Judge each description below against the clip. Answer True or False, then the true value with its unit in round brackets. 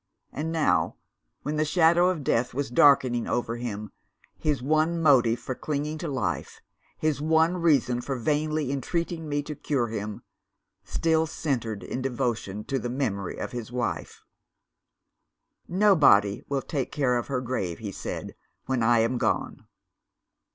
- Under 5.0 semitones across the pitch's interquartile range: True (4.5 semitones)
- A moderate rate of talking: True (150 wpm)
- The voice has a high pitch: False (135 Hz)